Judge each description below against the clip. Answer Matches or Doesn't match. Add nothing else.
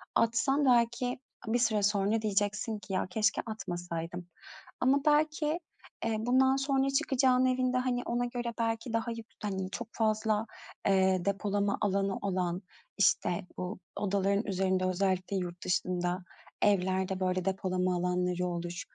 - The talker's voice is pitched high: Matches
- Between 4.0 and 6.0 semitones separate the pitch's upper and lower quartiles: Matches